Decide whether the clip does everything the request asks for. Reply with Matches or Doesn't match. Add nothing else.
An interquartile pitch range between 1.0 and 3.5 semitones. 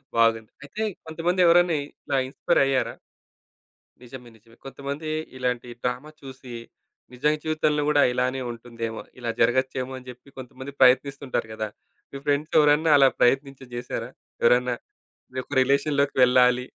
Matches